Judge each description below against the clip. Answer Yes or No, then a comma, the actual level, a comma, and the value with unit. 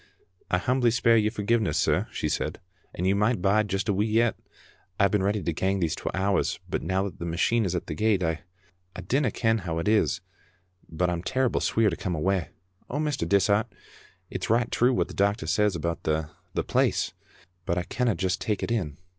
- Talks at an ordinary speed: No, fast, 215 wpm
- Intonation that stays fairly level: No, average, 3.9 semitones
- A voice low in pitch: Yes, low, 100 Hz